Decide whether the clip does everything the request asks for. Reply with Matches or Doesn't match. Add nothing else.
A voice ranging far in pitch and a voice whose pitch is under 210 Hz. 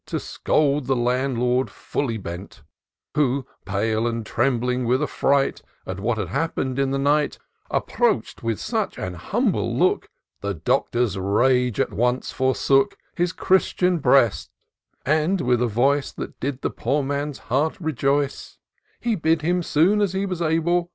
Doesn't match